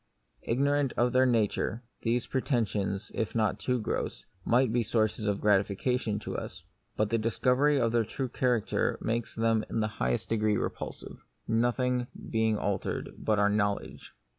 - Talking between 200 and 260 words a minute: No, average, 155 wpm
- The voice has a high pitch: No, low, 115 Hz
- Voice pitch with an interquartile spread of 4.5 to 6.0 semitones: No, average, 2.7 semitones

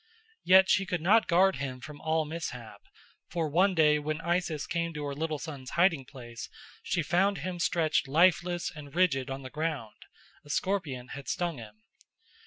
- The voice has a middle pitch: Yes, medium, 160 Hz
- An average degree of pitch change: Yes, average, 4.0 semitones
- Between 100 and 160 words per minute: No, average, 175 wpm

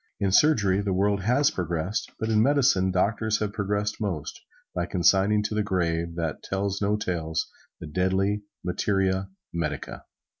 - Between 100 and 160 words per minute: Yes, average, 150 wpm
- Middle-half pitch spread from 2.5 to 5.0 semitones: Yes, average, 2.8 semitones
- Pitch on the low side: Yes, very low, 95 Hz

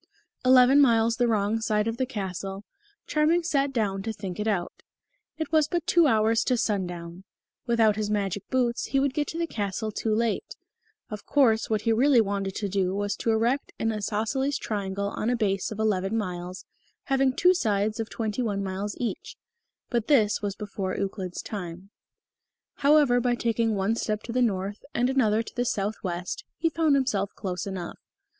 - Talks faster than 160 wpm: Yes, average, 180 wpm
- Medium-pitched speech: No, high, 220 Hz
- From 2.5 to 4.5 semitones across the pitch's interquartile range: Yes, average, 4.0 semitones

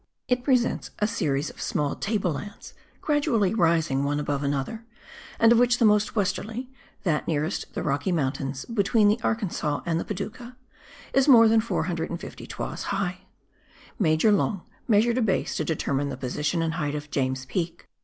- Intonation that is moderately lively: No, wide, 7.1 semitones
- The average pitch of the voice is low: No, medium, 185 Hz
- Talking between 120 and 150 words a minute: No, average, 165 wpm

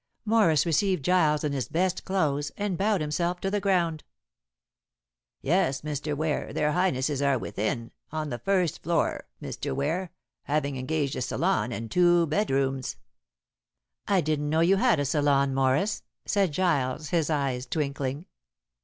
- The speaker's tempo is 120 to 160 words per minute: Yes, average, 145 wpm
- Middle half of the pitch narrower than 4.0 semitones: No, average, 4.5 semitones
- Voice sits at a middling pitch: Yes, medium, 155 Hz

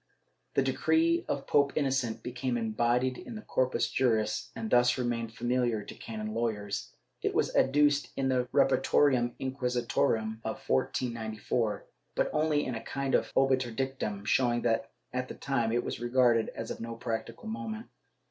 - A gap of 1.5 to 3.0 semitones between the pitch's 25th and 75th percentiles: Yes, average, 2.7 semitones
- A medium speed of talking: Yes, average, 155 wpm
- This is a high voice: No, low, 125 Hz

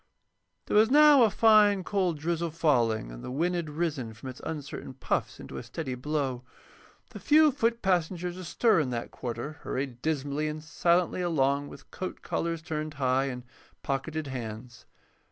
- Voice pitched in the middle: Yes, medium, 155 Hz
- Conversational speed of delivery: Yes, average, 165 wpm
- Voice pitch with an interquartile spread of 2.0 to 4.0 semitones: No, average, 5.1 semitones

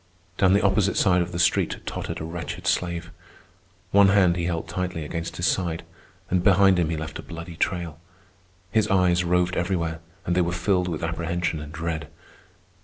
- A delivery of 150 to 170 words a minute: No, average, 180 wpm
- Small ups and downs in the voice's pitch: Yes, narrow, 1.7 semitones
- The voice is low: Yes, very low, 85 Hz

